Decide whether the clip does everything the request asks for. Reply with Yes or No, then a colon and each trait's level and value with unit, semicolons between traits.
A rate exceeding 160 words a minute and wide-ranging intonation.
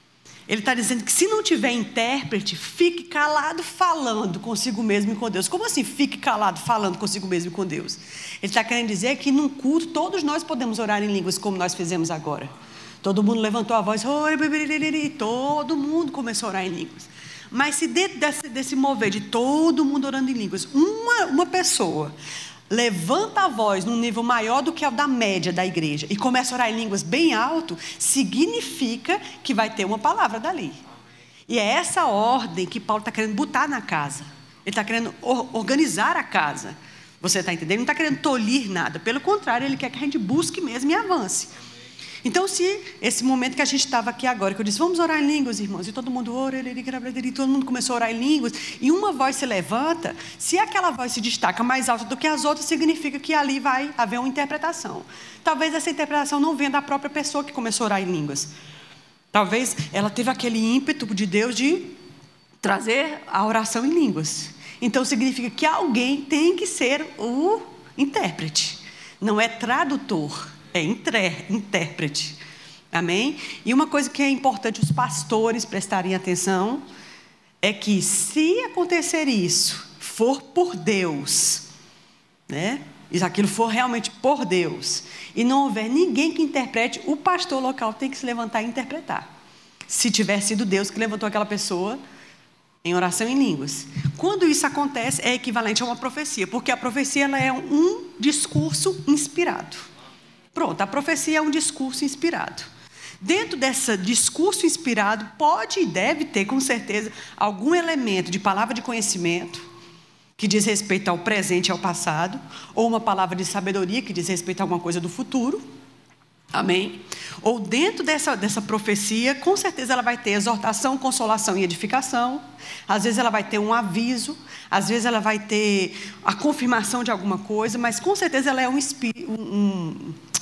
Yes: average, 175 wpm; wide, 6.3 semitones